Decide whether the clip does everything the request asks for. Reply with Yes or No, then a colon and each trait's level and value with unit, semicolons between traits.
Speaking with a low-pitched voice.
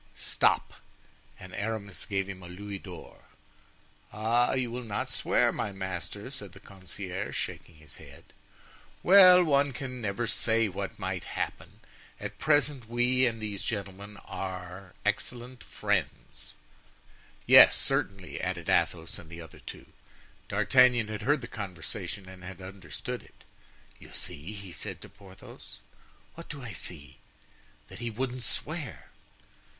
Yes: low, 105 Hz